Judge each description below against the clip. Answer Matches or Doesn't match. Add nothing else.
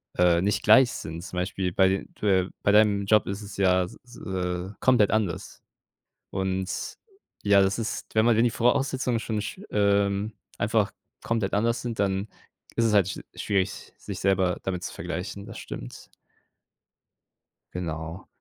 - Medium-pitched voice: Doesn't match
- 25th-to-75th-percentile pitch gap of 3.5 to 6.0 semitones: Doesn't match